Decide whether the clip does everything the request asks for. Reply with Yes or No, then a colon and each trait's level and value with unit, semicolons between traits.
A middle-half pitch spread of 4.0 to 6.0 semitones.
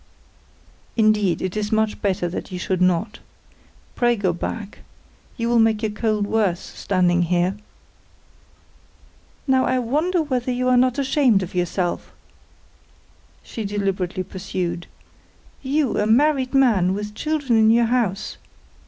Yes: average, 5.0 semitones